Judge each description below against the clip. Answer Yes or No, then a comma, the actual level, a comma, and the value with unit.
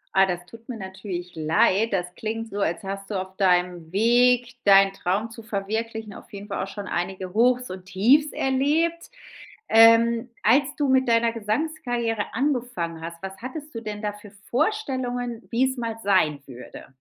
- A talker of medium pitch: No, high, 220 Hz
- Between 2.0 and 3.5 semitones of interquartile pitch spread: No, average, 4.3 semitones